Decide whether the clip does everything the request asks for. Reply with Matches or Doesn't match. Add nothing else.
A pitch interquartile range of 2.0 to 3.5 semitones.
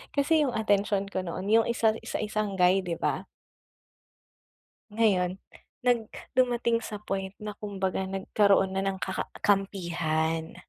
Matches